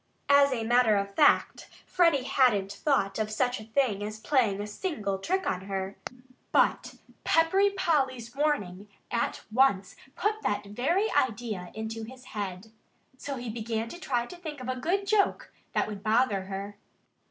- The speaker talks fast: No, average, 165 wpm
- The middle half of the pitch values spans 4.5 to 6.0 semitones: Yes, wide, 5.5 semitones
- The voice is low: No, high, 235 Hz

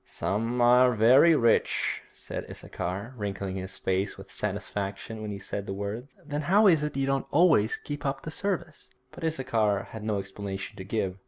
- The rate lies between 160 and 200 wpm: Yes, average, 180 wpm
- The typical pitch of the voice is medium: No, low, 115 Hz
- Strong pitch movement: Yes, wide, 6.0 semitones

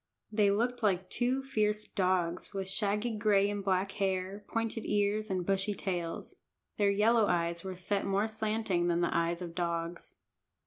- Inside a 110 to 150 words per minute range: No, average, 165 wpm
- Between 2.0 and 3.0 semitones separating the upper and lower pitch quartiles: Yes, average, 2.7 semitones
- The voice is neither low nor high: No, high, 200 Hz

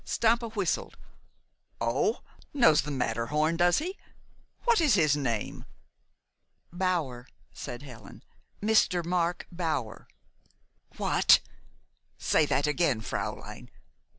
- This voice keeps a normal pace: No, slow, 95 wpm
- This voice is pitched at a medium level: Yes, medium, 160 Hz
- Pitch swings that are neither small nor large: No, wide, 6.0 semitones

